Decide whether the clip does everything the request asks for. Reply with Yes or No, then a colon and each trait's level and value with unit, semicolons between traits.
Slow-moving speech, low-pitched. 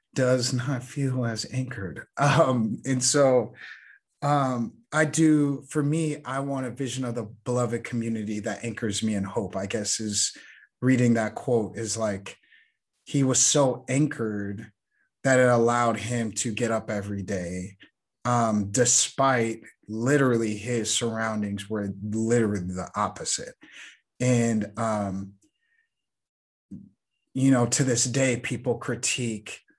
Yes: slow, 130 wpm; low, 120 Hz